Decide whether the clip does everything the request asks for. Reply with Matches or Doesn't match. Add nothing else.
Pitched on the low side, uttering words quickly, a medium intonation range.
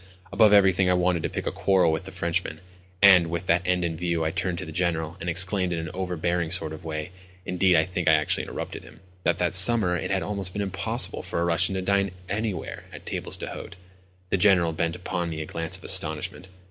Doesn't match